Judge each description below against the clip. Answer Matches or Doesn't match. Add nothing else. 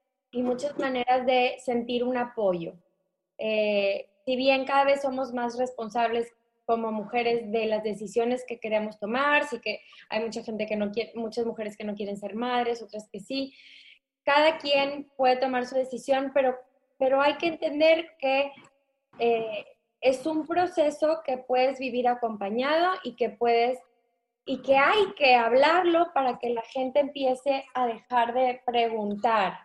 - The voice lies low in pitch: Doesn't match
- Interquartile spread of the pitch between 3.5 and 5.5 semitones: Doesn't match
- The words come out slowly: Doesn't match